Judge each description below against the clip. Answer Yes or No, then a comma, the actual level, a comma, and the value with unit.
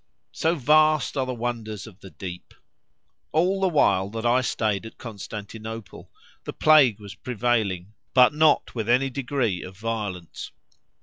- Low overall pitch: Yes, low, 115 Hz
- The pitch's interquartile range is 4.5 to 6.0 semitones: Yes, average, 4.8 semitones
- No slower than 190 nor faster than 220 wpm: No, average, 145 wpm